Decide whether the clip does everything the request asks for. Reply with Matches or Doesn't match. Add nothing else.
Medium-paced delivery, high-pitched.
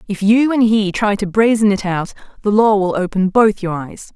Doesn't match